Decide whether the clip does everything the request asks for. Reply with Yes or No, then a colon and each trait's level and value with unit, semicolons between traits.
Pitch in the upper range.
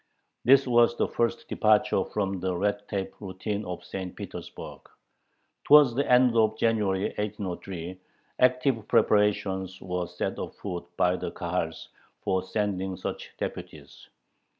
No: low, 100 Hz